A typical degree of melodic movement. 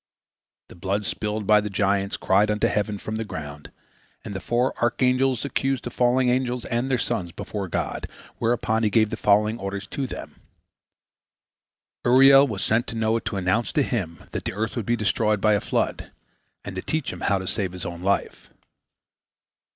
Yes: average, 3.5 semitones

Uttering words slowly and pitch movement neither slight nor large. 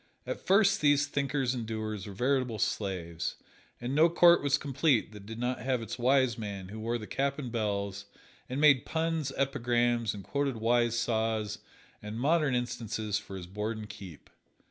No: average, 175 wpm; average, 4.5 semitones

